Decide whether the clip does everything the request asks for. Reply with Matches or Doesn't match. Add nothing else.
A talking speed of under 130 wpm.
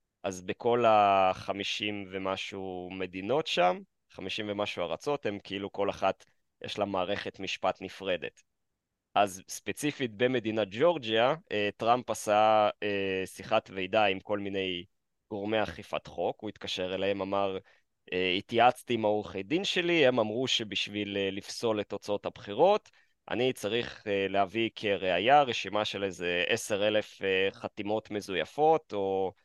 Matches